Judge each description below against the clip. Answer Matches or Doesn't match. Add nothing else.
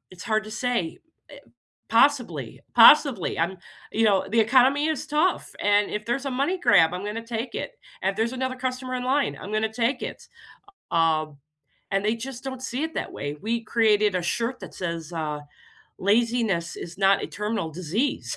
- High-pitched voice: Matches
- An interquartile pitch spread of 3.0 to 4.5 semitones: Doesn't match